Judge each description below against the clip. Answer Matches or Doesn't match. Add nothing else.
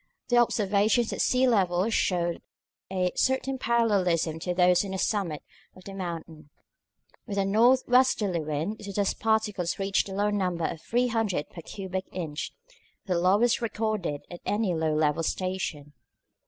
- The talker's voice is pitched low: Doesn't match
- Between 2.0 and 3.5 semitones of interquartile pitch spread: Doesn't match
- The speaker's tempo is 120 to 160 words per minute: Matches